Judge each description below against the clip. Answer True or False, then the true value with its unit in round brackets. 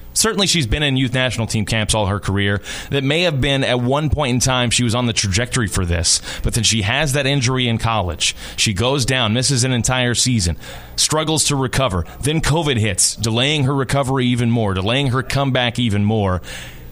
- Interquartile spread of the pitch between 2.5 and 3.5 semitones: False (4.2 semitones)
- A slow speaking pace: False (205 wpm)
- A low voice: True (120 Hz)